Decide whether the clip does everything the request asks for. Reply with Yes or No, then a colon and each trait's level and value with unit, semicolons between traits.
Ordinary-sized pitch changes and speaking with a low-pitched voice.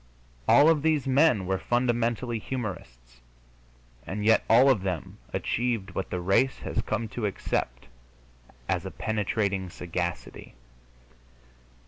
Yes: average, 4.9 semitones; low, 110 Hz